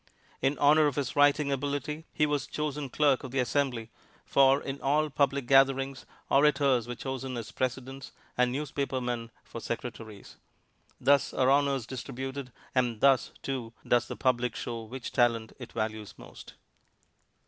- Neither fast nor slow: Yes, average, 150 wpm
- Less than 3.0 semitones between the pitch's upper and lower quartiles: Yes, narrow, 2.5 semitones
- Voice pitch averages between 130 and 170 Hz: Yes, low, 135 Hz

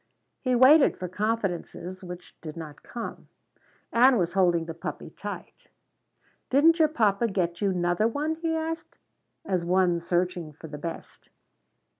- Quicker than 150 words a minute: No, average, 145 wpm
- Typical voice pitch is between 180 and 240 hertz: Yes, medium, 185 Hz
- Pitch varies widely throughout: Yes, wide, 6.5 semitones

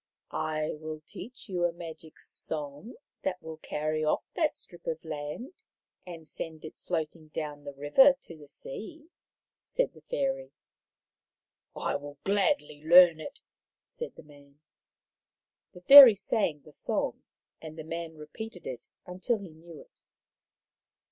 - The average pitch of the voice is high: No, medium, 160 Hz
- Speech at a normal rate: Yes, average, 150 wpm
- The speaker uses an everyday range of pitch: Yes, average, 4.8 semitones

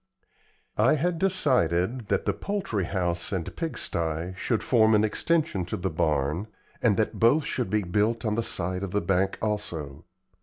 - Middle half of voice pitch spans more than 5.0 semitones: Yes, wide, 5.6 semitones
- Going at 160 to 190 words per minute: Yes, average, 165 wpm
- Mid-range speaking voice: No, low, 105 Hz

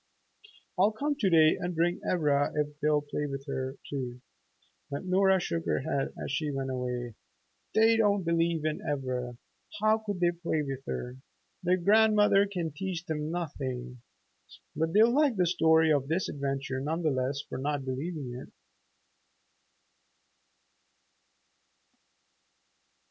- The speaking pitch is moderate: Yes, medium, 155 Hz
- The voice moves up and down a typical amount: Yes, average, 5.0 semitones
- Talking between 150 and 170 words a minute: No, average, 140 wpm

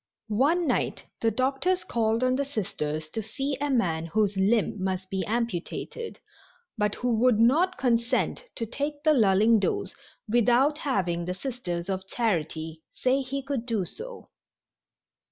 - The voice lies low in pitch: No, high, 230 Hz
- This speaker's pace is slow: No, average, 150 wpm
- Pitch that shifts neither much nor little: No, wide, 6.0 semitones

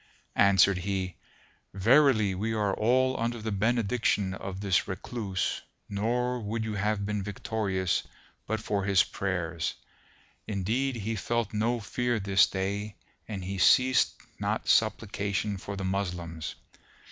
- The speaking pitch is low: Yes, low, 100 Hz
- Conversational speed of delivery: No, slow, 130 wpm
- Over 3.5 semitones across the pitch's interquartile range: No, average, 2.8 semitones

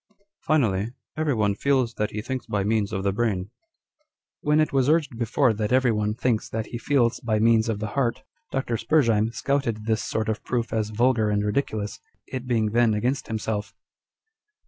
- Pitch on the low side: Yes, low, 115 Hz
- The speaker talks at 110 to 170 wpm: No, average, 190 wpm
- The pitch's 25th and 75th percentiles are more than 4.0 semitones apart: No, average, 3.4 semitones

